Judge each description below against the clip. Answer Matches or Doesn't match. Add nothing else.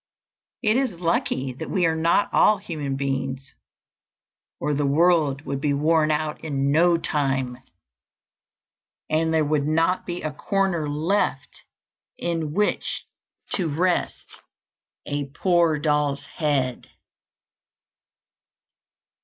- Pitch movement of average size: Matches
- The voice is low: Doesn't match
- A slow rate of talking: Matches